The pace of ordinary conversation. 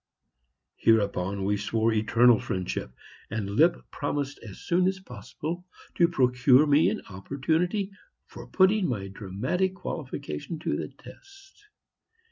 No: slow, 120 wpm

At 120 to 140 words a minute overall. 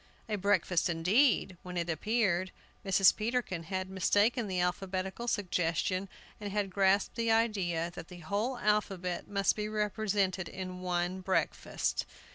Yes: slow, 135 wpm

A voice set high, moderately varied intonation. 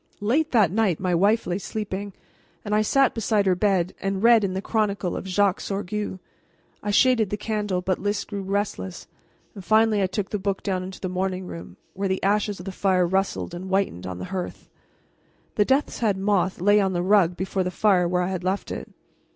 No: high, 195 Hz; narrow, 2.1 semitones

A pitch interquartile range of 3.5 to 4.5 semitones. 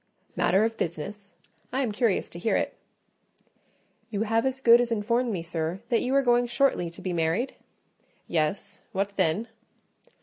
No: wide, 5.4 semitones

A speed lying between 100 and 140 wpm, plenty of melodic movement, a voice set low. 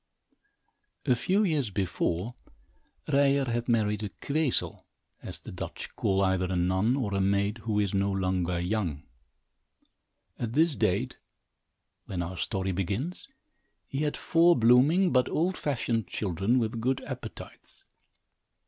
Yes: slow, 135 wpm; wide, 6.0 semitones; low, 110 Hz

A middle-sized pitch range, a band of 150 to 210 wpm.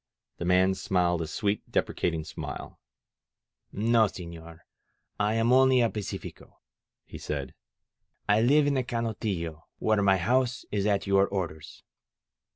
No: average, 4.8 semitones; slow, 135 wpm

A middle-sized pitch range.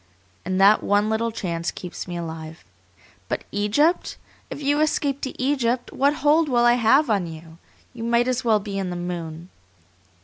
No: wide, 6.7 semitones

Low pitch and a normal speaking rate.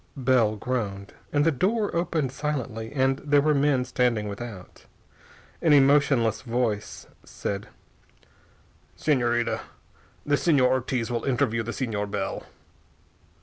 No: low, 125 Hz; slow, 115 wpm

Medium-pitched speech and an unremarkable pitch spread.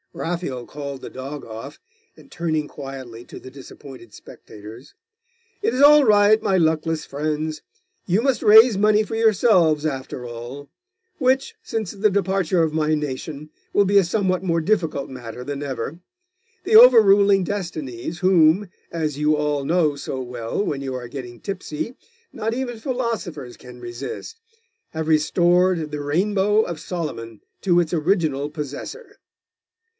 No: medium, 160 Hz; wide, 6.3 semitones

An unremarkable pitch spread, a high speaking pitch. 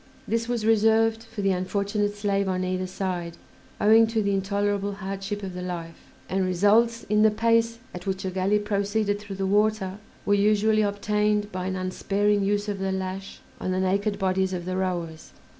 No: narrow, 2.0 semitones; high, 200 Hz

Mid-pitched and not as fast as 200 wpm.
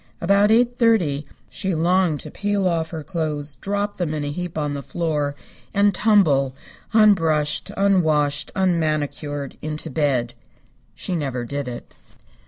Yes: medium, 160 Hz; average, 140 wpm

